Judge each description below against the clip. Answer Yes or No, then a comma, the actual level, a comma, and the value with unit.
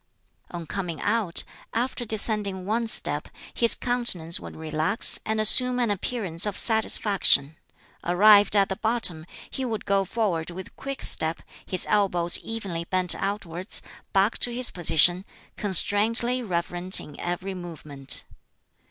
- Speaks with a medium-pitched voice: No, high, 195 Hz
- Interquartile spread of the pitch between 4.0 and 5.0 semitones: Yes, average, 4.3 semitones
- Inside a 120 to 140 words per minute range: Yes, slow, 135 wpm